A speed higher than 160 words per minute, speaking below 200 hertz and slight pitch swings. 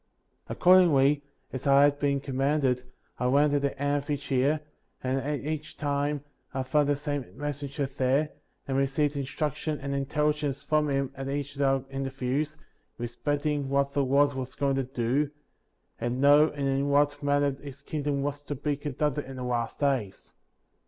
Yes: average, 180 wpm; medium, 140 Hz; narrow, 1.4 semitones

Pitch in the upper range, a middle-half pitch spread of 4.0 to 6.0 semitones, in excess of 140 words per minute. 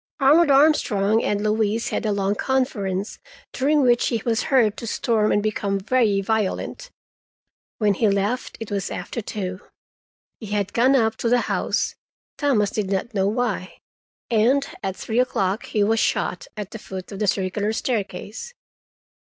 No: high, 215 Hz; average, 3.5 semitones; average, 155 wpm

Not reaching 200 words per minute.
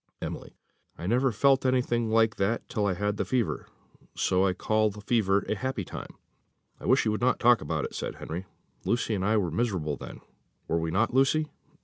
No: fast, 205 wpm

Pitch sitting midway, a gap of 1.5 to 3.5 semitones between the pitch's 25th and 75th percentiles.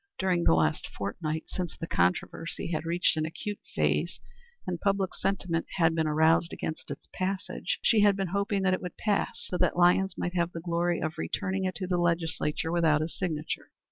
Yes: medium, 175 Hz; average, 2.7 semitones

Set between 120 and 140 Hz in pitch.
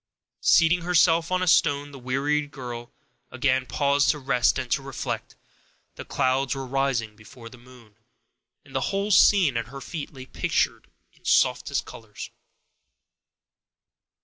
Yes: low, 135 Hz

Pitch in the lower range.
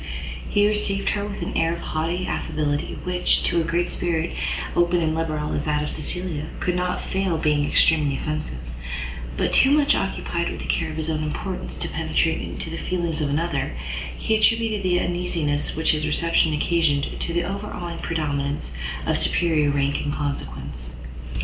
No: medium, 160 Hz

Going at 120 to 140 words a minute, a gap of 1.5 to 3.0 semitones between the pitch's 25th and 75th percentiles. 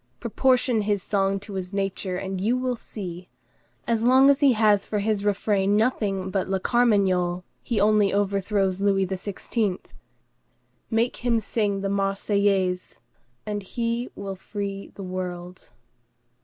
Yes: slow, 135 wpm; narrow, 2.4 semitones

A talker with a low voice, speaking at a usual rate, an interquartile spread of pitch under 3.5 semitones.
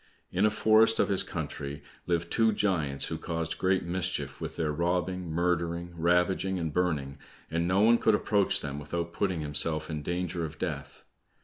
Yes: very low, 85 Hz; average, 175 wpm; average, 2.9 semitones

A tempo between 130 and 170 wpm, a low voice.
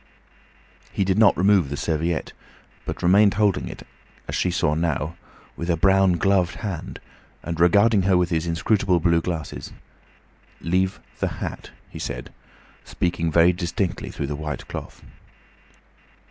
Yes: average, 145 wpm; very low, 90 Hz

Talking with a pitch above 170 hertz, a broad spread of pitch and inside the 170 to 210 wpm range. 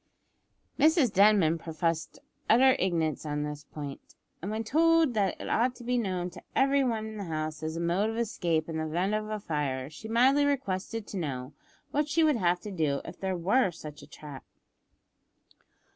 Yes: high, 190 Hz; wide, 6.7 semitones; average, 190 wpm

